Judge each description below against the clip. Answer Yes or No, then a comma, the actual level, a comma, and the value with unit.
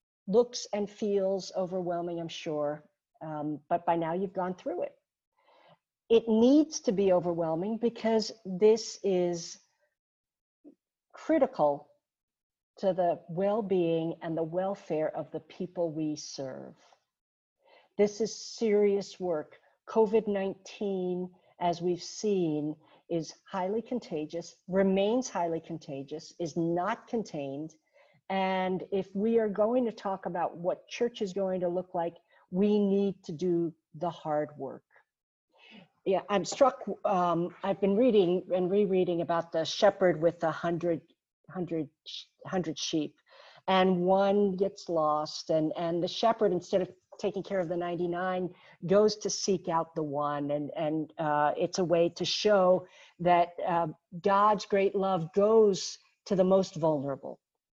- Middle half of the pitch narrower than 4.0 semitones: Yes, average, 3.3 semitones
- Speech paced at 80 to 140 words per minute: Yes, slow, 135 wpm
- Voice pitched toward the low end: No, medium, 185 Hz